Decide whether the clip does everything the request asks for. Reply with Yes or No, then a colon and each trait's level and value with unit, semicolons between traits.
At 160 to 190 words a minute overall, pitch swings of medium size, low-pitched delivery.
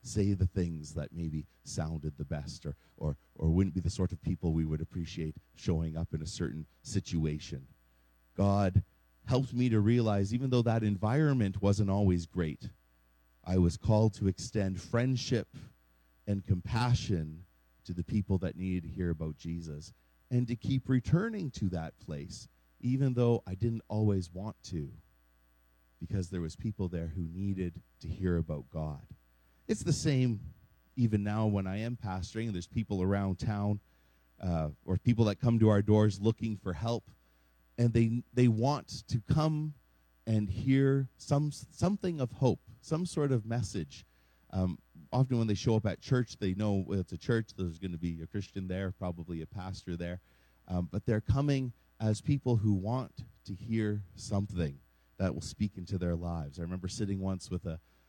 No: average, 175 wpm; wide, 5.7 semitones; very low, 95 Hz